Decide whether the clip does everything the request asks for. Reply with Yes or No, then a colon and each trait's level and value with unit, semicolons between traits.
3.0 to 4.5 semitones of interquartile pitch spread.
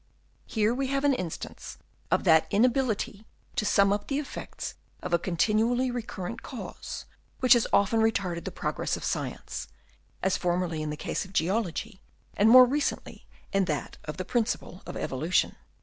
No: average, 5.3 semitones